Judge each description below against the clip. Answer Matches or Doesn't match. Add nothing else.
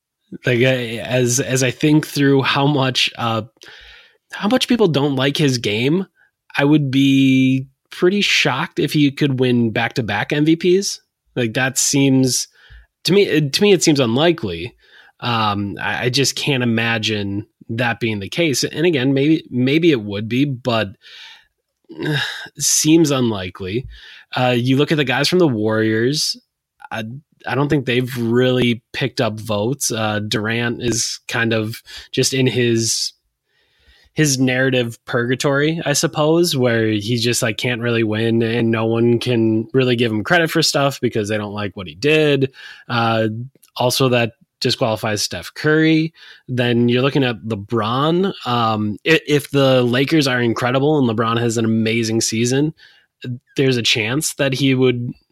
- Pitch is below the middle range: Matches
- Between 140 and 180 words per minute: Matches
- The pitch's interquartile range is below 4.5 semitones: Matches